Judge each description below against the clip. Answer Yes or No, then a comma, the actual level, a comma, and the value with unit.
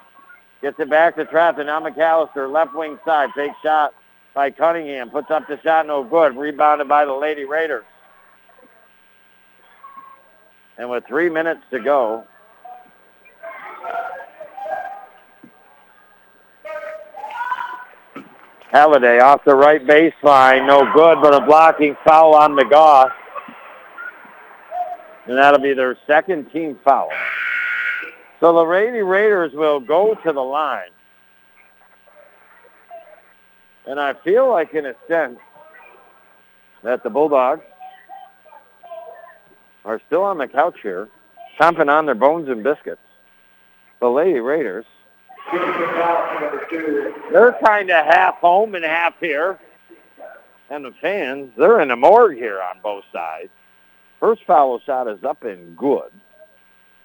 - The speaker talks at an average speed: No, slow, 115 wpm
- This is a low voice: No, medium, 160 Hz